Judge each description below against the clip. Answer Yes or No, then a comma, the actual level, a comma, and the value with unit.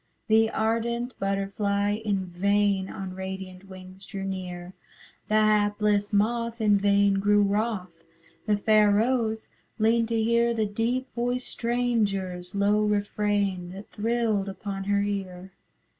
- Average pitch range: No, narrow, 2.2 semitones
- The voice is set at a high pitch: Yes, high, 205 Hz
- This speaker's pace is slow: Yes, slow, 130 wpm